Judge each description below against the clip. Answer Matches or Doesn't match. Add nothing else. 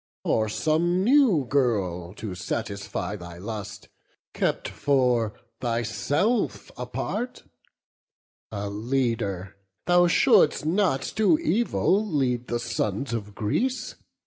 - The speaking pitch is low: Matches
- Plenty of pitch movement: Matches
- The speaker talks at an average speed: Doesn't match